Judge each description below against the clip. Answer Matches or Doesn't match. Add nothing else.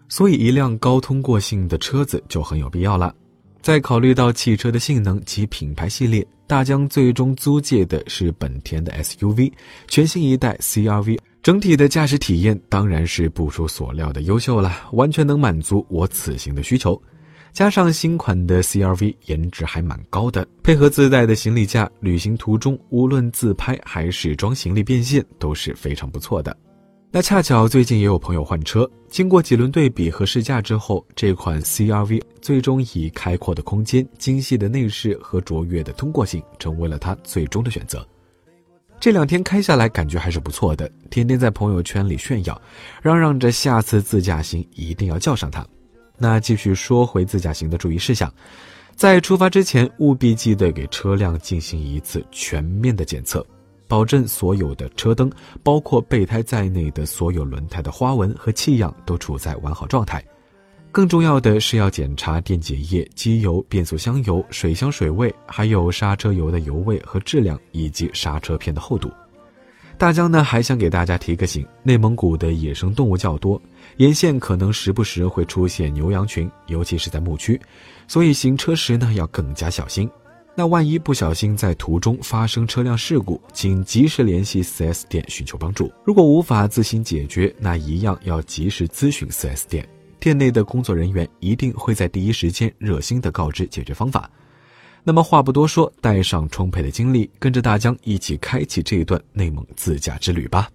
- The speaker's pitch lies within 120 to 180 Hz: Doesn't match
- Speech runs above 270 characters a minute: Matches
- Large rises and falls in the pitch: Matches